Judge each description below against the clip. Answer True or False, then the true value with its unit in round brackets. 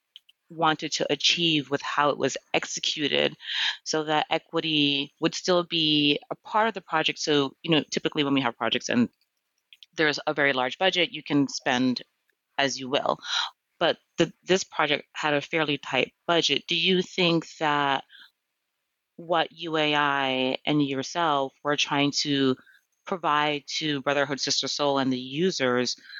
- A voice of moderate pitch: True (150 Hz)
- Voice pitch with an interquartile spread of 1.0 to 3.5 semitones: True (2.9 semitones)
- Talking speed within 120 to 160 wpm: True (155 wpm)